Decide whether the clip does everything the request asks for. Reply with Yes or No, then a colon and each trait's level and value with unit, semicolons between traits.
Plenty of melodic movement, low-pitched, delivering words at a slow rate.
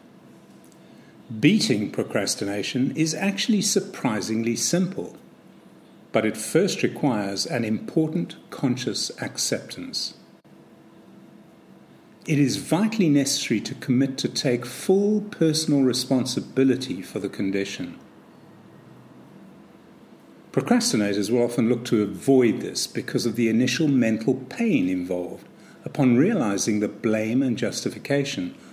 Yes: wide, 6.0 semitones; low, 130 Hz; slow, 100 wpm